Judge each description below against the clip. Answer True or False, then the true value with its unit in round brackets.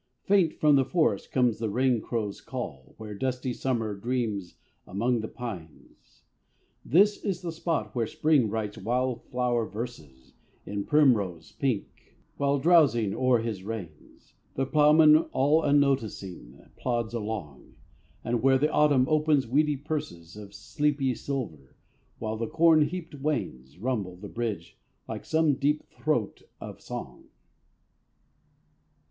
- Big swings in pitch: True (5.7 semitones)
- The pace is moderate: False (130 wpm)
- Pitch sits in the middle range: False (125 Hz)